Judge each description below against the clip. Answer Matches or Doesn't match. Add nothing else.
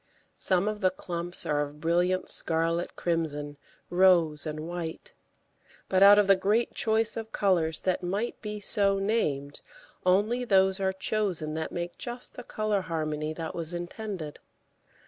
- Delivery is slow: Doesn't match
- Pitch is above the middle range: Doesn't match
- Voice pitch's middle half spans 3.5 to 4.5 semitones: Matches